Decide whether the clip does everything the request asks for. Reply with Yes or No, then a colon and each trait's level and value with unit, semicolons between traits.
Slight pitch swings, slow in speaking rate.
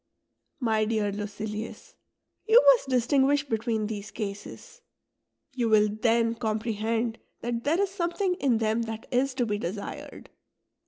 No: average, 3.4 semitones; slow, 130 wpm